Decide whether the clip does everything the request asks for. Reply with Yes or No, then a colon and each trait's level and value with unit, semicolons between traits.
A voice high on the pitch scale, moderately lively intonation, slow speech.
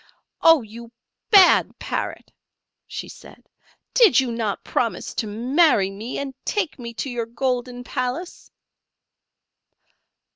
Yes: high, 245 Hz; average, 4.1 semitones; slow, 115 wpm